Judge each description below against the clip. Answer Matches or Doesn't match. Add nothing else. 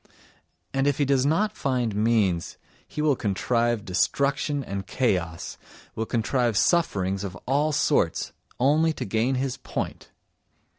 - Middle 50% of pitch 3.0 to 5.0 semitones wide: Doesn't match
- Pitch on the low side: Matches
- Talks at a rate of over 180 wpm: Doesn't match